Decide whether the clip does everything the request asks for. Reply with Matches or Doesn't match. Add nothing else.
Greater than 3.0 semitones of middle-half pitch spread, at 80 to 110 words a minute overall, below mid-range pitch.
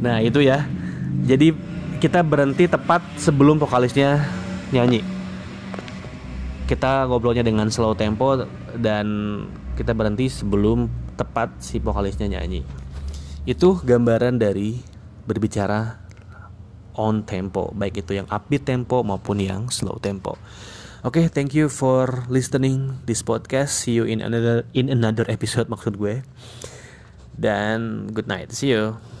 Doesn't match